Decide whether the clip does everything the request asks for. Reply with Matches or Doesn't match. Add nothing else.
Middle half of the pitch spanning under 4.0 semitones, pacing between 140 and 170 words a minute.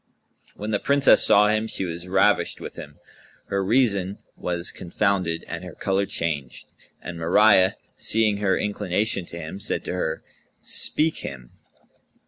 Matches